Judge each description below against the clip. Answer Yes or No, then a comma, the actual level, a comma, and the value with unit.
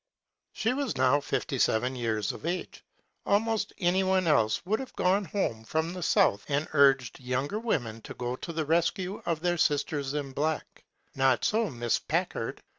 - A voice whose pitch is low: No, medium, 155 Hz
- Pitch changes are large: Yes, wide, 6.3 semitones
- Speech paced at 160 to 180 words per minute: Yes, average, 175 wpm